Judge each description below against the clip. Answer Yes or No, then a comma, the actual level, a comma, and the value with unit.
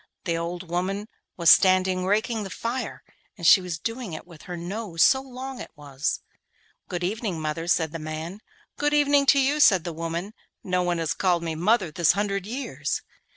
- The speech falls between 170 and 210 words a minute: Yes, average, 195 wpm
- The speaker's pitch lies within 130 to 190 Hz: Yes, medium, 185 Hz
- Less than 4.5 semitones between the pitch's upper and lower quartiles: No, average, 4.8 semitones